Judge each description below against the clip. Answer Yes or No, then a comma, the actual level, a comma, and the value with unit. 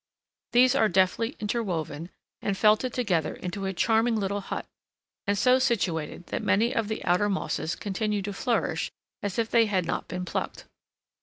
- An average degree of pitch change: Yes, average, 3.6 semitones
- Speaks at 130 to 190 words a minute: Yes, average, 165 wpm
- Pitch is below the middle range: No, high, 205 Hz